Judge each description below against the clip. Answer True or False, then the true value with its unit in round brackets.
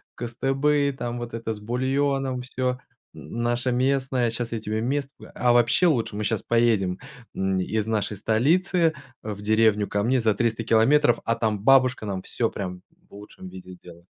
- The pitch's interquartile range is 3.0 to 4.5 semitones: True (3.4 semitones)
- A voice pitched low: True (115 Hz)